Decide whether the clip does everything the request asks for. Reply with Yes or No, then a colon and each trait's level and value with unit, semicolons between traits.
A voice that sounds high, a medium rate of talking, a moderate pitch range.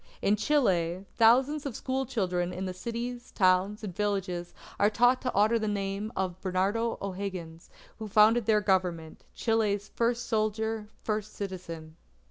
Yes: high, 205 Hz; average, 145 wpm; average, 3.5 semitones